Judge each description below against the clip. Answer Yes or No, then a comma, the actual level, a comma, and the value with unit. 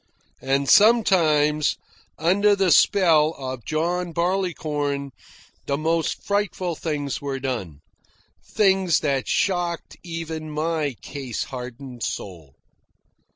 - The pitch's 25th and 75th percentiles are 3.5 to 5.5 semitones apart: Yes, average, 4.2 semitones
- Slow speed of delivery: Yes, slow, 100 wpm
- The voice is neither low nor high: Yes, medium, 155 Hz